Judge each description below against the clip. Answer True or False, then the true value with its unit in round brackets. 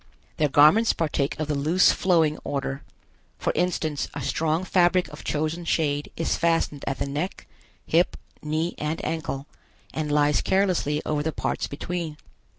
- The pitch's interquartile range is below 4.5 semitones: True (2.5 semitones)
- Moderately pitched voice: True (155 Hz)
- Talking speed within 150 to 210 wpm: True (155 wpm)